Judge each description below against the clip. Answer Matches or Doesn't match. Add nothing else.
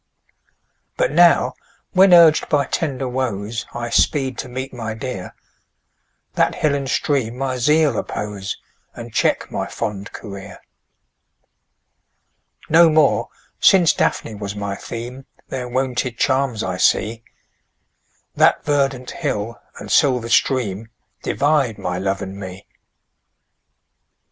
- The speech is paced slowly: Matches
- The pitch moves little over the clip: Doesn't match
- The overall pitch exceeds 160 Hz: Doesn't match